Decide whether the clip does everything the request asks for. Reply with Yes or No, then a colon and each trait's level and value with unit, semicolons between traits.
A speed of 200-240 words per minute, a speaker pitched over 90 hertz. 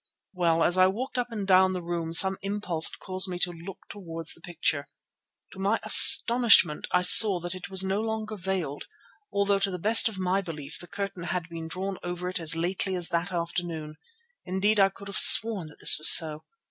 Yes: fast, 205 wpm; medium, 185 Hz